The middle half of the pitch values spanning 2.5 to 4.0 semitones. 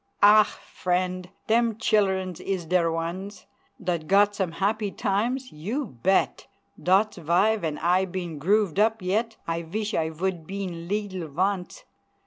Yes: average, 3.4 semitones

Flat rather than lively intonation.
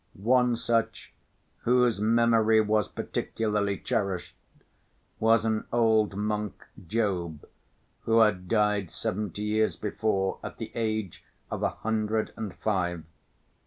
Yes: narrow, 1.8 semitones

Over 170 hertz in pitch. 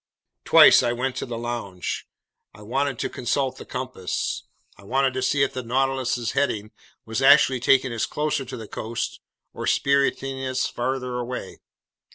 No: low, 130 Hz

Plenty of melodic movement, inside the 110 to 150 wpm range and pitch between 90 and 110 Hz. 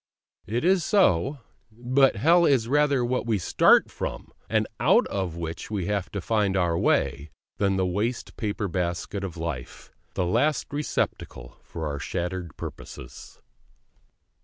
Yes: wide, 6.6 semitones; average, 145 wpm; low, 100 Hz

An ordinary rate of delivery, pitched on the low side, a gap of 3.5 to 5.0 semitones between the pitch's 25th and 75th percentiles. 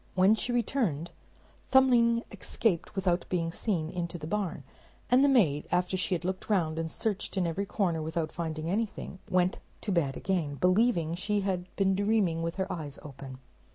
No: average, 175 wpm; medium, 180 Hz; average, 3.9 semitones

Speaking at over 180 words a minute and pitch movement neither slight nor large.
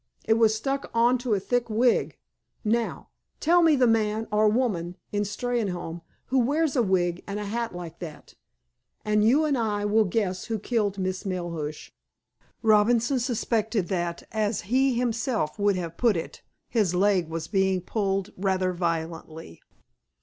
No: average, 155 wpm; average, 4.3 semitones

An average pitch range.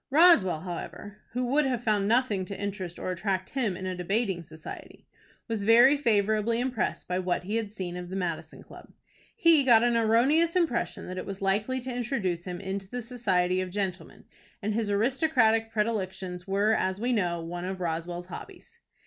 Yes: average, 4.6 semitones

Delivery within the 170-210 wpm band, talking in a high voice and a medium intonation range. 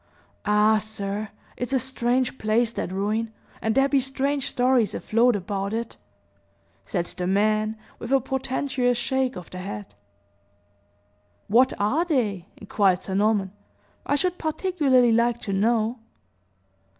No: slow, 135 wpm; high, 230 Hz; average, 4.3 semitones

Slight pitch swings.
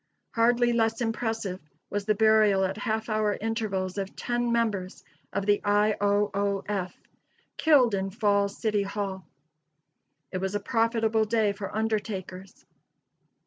Yes: narrow, 2.2 semitones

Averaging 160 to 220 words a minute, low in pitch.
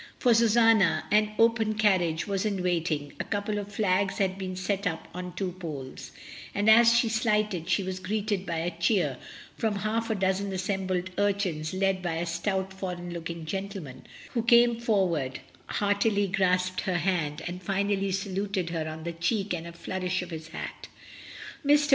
No: average, 180 wpm; high, 190 Hz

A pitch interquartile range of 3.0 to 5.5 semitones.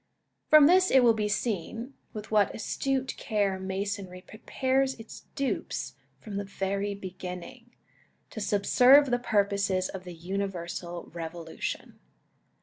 Yes: average, 4.5 semitones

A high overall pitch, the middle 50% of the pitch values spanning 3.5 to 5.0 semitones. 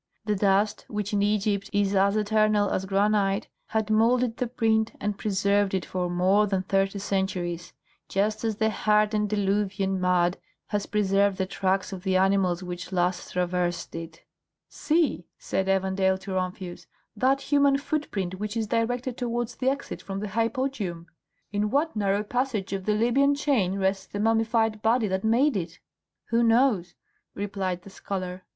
No: high, 205 Hz; average, 2.7 semitones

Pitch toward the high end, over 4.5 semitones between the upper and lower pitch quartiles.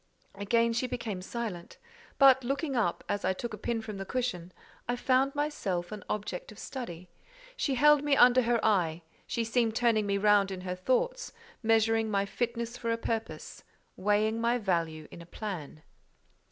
No: high, 225 Hz; average, 4.0 semitones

